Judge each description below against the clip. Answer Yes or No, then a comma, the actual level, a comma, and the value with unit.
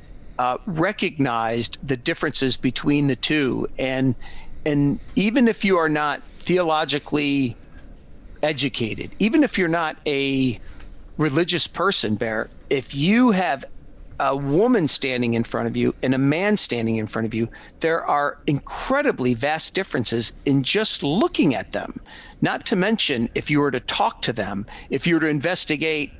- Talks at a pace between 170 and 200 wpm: No, average, 155 wpm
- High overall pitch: No, medium, 140 Hz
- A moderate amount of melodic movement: No, wide, 5.7 semitones